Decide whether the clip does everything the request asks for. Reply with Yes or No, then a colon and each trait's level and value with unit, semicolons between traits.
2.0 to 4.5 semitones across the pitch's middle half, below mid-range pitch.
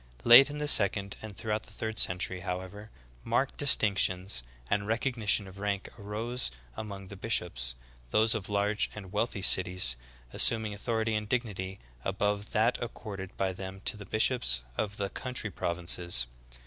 Yes: average, 2.8 semitones; low, 105 Hz